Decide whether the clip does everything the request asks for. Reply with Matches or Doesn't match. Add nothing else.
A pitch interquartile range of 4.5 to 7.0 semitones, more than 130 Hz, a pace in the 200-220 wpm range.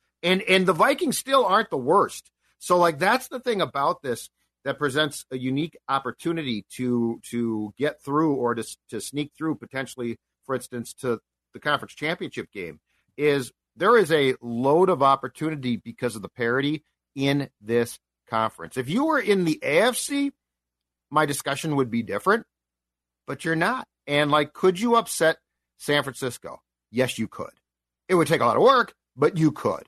Doesn't match